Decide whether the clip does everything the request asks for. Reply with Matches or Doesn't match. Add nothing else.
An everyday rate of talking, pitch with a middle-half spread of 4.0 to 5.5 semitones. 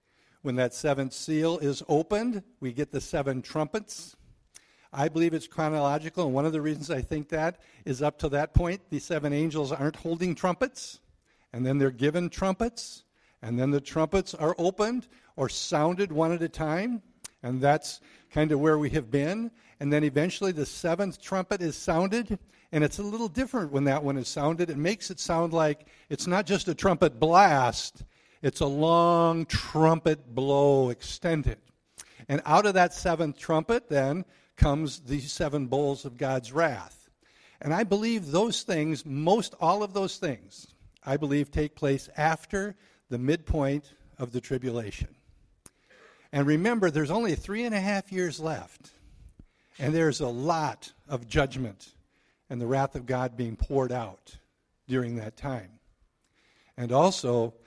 Matches